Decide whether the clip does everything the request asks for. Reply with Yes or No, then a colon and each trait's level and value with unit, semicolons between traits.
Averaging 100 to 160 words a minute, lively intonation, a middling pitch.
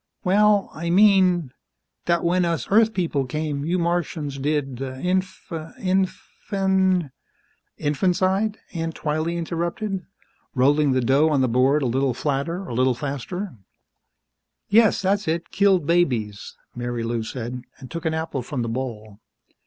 Yes: slow, 135 wpm; wide, 5.7 semitones; medium, 160 Hz